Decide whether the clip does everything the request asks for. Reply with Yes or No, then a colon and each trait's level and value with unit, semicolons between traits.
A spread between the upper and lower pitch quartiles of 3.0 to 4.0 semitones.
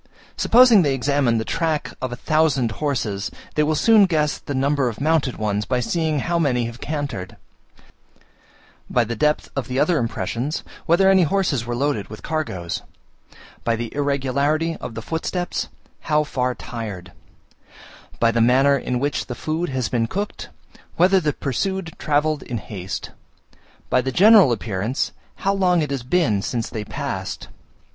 No: average, 5.1 semitones